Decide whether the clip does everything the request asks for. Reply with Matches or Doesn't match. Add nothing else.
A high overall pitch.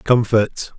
Doesn't match